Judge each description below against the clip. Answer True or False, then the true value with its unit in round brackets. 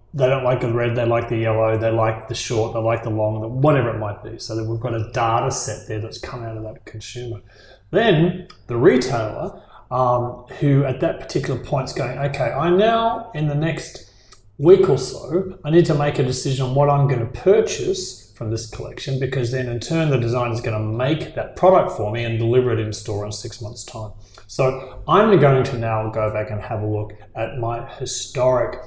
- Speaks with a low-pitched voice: True (120 Hz)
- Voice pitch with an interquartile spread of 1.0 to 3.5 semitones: False (4.0 semitones)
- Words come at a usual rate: False (220 wpm)